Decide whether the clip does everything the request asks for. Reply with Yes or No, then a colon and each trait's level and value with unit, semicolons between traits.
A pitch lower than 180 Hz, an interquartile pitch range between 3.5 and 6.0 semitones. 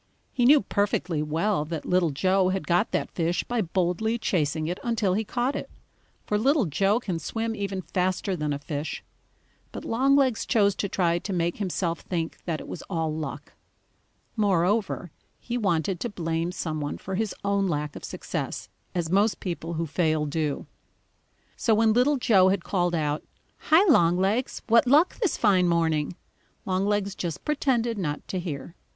No: medium, 185 Hz; average, 4.8 semitones